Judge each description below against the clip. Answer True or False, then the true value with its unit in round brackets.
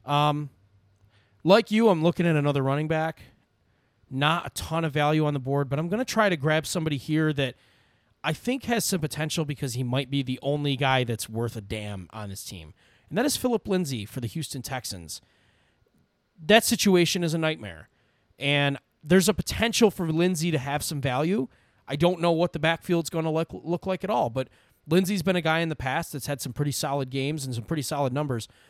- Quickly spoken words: True (210 wpm)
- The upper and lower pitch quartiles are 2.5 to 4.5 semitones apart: False (4.9 semitones)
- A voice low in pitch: False (145 Hz)